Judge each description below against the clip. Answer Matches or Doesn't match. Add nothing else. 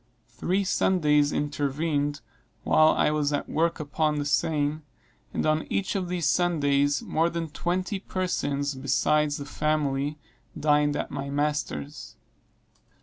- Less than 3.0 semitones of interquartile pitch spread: Matches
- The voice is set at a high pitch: Doesn't match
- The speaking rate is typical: Doesn't match